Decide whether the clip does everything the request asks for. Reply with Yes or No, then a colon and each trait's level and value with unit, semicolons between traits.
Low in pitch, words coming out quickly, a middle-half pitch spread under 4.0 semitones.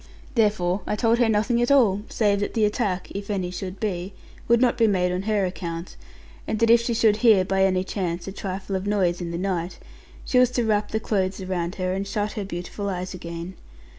No: high, 195 Hz; fast, 225 wpm; average, 2.9 semitones